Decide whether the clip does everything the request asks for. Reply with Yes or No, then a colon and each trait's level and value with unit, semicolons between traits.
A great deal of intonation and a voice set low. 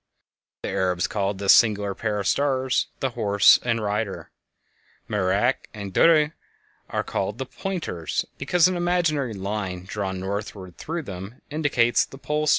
Yes: wide, 6.5 semitones; low, 110 Hz